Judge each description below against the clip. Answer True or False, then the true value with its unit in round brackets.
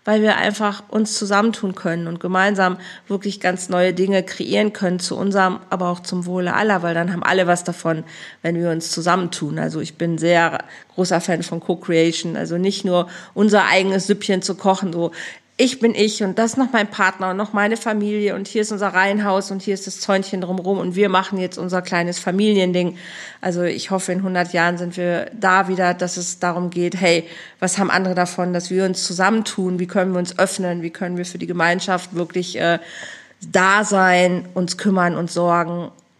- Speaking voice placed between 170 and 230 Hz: True (185 Hz)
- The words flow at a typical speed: False (200 wpm)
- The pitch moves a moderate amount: False (1.9 semitones)